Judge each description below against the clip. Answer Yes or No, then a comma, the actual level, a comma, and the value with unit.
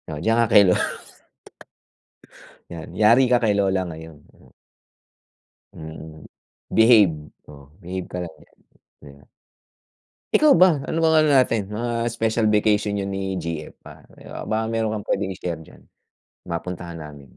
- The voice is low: Yes, low, 100 Hz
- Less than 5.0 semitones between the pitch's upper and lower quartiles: No, average, 5.3 semitones